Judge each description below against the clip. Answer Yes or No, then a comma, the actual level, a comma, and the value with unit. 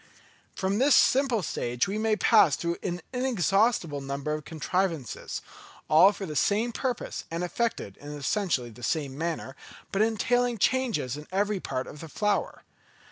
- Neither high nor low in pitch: Yes, medium, 180 Hz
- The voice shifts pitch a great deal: Yes, wide, 6.8 semitones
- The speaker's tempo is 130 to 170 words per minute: Yes, average, 155 wpm